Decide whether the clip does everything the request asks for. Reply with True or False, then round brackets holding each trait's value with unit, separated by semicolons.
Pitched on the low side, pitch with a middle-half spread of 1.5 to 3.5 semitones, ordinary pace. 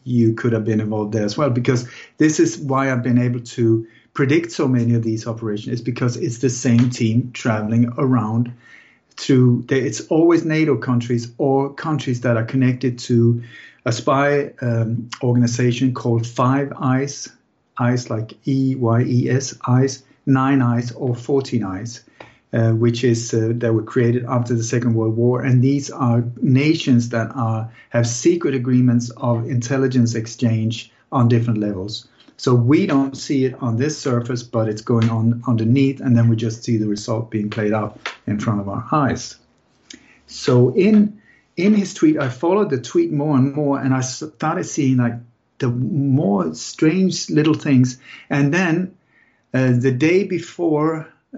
True (125 Hz; 2.9 semitones; 165 wpm)